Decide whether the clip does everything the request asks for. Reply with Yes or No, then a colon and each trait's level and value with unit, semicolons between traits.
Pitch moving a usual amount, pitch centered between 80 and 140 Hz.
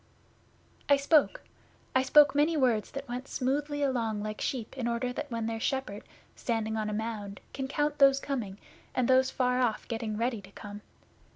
No: average, 3.8 semitones; very high, 250 Hz